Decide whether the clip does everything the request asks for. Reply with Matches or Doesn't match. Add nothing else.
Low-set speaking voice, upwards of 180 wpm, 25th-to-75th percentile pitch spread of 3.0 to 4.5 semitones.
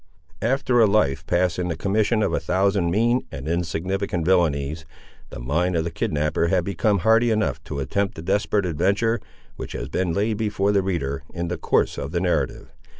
Matches